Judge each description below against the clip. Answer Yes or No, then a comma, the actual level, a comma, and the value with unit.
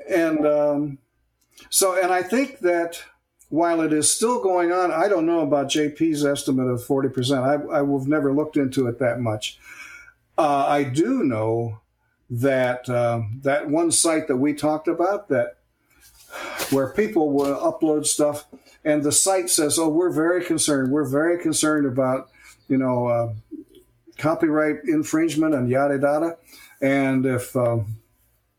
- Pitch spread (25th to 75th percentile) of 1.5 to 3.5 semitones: No, average, 4.0 semitones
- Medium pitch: Yes, medium, 145 Hz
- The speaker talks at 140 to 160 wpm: Yes, average, 150 wpm